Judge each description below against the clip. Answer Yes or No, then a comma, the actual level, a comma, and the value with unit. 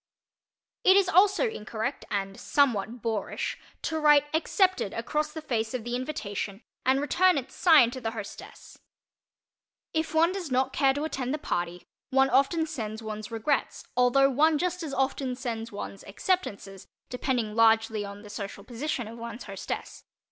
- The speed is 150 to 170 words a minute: Yes, average, 160 wpm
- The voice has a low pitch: No, very high, 250 Hz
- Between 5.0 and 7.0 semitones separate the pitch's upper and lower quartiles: Yes, wide, 5.6 semitones